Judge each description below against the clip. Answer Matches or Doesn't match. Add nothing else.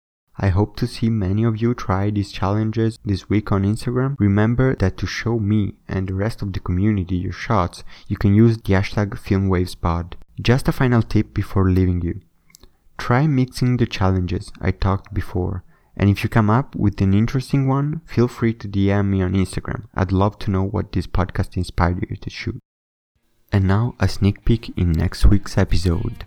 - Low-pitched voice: Matches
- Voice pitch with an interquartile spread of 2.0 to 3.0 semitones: Doesn't match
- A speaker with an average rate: Matches